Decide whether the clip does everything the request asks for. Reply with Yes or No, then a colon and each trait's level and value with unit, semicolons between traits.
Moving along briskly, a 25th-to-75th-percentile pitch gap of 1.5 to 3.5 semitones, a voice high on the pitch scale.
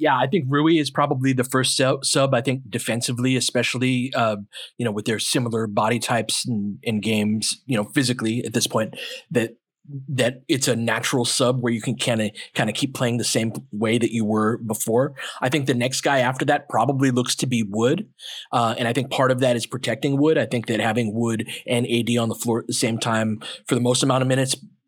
No: fast, 225 wpm; narrow, 2.6 semitones; low, 120 Hz